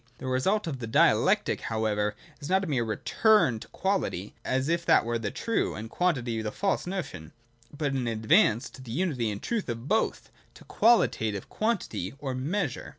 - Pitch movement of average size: No, wide, 8.4 semitones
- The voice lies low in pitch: Yes, low, 130 Hz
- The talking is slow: No, average, 180 wpm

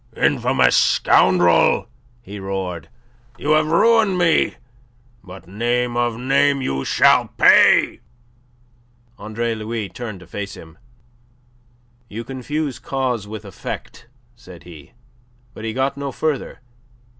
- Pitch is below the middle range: Yes, low, 115 Hz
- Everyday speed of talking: No, slow, 120 wpm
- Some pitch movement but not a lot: No, wide, 5.7 semitones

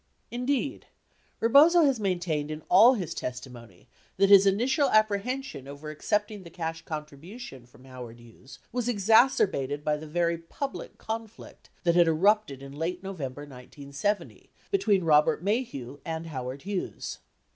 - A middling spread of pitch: No, wide, 7.1 semitones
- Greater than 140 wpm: No, slow, 135 wpm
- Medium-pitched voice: Yes, medium, 170 Hz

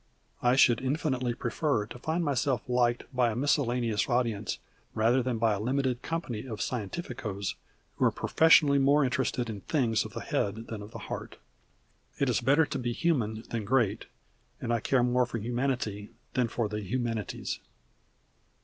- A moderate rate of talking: Yes, average, 165 wpm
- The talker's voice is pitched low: Yes, low, 120 Hz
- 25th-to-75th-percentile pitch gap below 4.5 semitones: Yes, average, 3.1 semitones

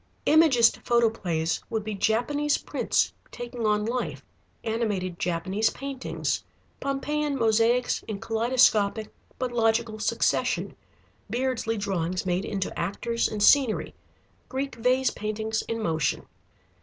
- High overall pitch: Yes, high, 225 Hz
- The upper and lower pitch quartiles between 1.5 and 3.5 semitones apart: Yes, average, 3.2 semitones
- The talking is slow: Yes, slow, 110 wpm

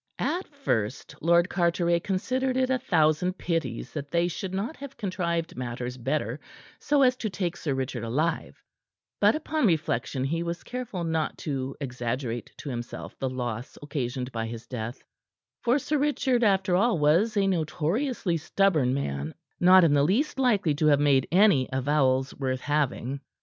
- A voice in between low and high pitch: Yes, medium, 160 Hz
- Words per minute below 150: No, average, 160 wpm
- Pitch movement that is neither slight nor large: No, wide, 6.9 semitones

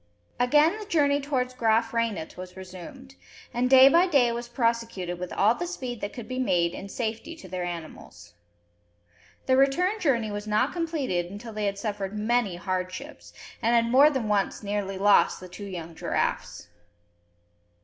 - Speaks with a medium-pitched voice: No, high, 230 Hz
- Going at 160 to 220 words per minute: Yes, average, 170 wpm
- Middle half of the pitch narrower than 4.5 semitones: No, wide, 5.4 semitones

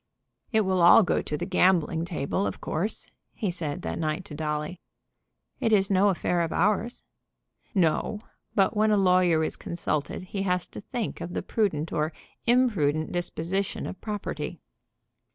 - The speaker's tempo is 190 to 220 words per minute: No, average, 160 wpm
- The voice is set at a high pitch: No, medium, 180 Hz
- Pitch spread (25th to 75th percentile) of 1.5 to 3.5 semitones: No, average, 4.0 semitones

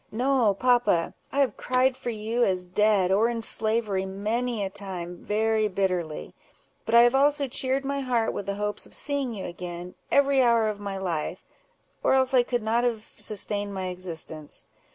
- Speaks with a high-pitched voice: Yes, high, 215 Hz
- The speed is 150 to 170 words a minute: No, average, 180 wpm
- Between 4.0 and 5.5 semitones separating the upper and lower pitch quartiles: Yes, average, 4.3 semitones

